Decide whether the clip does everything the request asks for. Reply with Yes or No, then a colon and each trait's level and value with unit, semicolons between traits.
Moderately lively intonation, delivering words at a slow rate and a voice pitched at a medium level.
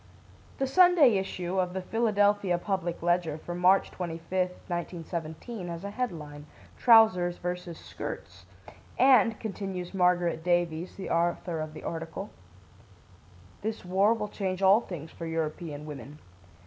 Yes: average, 3.2 semitones; slow, 130 wpm; medium, 180 Hz